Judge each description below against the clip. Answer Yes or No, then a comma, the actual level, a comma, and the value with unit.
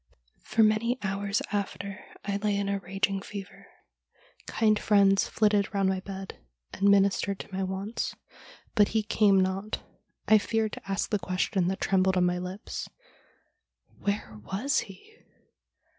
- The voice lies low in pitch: No, high, 200 Hz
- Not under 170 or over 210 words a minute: No, average, 155 wpm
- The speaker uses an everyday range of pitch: No, narrow, 1.6 semitones